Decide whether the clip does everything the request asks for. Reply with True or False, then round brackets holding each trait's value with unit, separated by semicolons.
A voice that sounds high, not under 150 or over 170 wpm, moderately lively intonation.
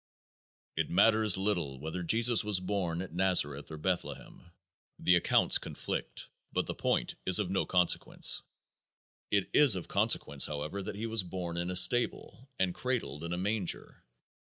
False (90 Hz; 155 wpm; 3.3 semitones)